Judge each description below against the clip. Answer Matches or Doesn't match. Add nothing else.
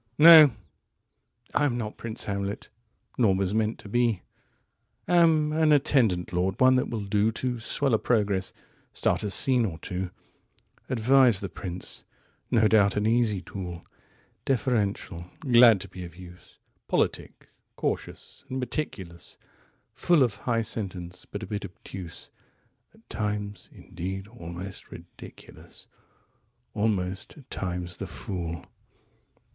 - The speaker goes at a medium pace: Doesn't match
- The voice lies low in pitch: Matches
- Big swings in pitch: Doesn't match